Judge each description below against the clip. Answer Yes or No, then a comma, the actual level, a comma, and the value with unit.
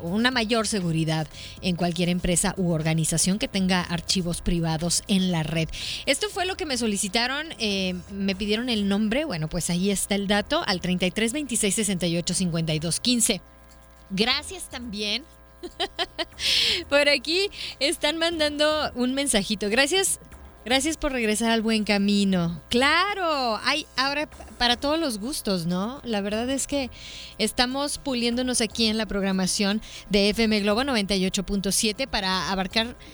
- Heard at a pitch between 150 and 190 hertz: No, high, 215 Hz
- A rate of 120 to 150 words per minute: Yes, average, 135 wpm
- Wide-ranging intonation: Yes, wide, 6.2 semitones